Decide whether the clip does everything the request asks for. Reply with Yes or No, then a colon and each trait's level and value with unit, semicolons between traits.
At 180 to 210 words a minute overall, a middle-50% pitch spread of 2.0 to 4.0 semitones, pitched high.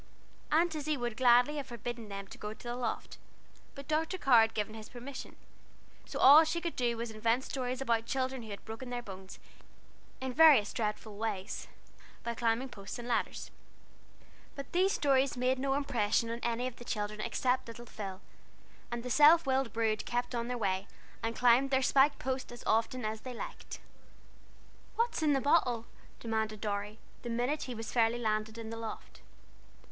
Yes: average, 185 wpm; average, 3.1 semitones; high, 240 Hz